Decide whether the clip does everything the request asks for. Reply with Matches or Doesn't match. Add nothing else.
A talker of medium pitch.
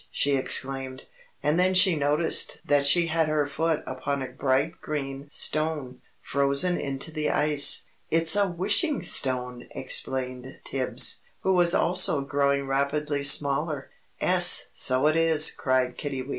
Matches